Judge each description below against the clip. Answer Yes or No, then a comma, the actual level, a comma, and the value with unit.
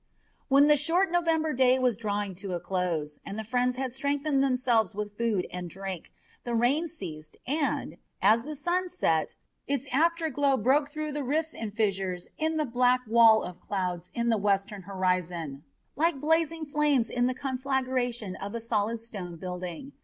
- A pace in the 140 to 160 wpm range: No, average, 175 wpm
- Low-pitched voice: No, high, 240 Hz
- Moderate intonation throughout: No, wide, 6.6 semitones